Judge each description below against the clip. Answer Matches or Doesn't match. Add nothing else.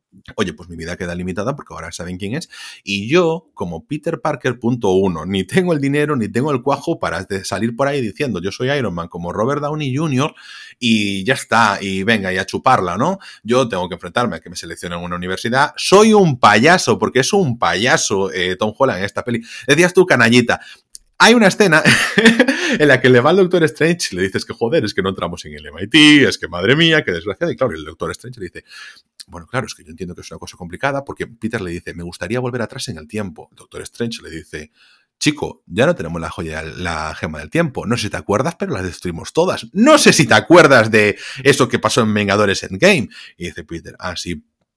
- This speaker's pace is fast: Matches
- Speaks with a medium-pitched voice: Doesn't match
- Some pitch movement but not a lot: Doesn't match